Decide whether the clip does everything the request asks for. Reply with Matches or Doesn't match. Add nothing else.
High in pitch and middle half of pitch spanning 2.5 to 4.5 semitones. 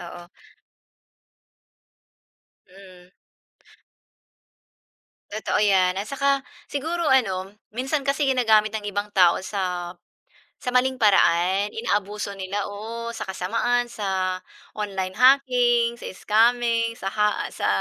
Matches